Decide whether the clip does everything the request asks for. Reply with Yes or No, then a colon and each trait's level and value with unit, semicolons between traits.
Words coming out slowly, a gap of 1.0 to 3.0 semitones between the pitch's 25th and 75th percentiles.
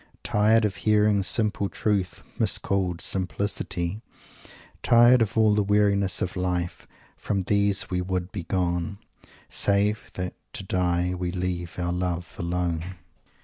Yes: slow, 125 wpm; narrow, 2.6 semitones